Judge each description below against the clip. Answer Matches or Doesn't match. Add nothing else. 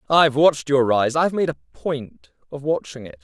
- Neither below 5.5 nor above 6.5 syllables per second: Matches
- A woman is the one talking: Doesn't match